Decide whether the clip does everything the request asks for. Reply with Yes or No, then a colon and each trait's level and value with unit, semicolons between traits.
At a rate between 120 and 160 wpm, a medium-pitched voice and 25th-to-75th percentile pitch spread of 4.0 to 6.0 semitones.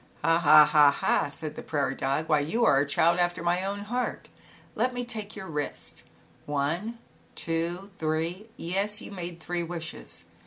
No: average, 170 wpm; medium, 170 Hz; average, 4.5 semitones